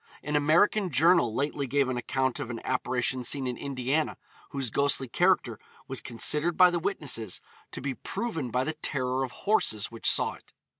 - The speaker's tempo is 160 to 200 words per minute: Yes, average, 180 wpm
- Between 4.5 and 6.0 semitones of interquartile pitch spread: No, average, 3.6 semitones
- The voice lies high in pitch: No, low, 135 Hz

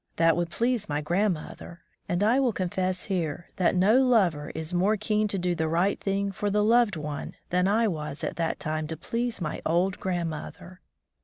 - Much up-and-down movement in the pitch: No, average, 4.1 semitones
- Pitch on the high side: No, medium, 180 Hz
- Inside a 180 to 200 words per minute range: Yes, average, 190 wpm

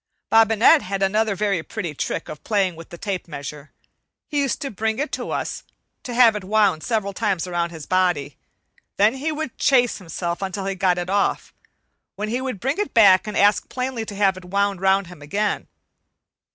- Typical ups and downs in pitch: Yes, average, 3.7 semitones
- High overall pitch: Yes, high, 200 Hz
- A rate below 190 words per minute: No, average, 195 wpm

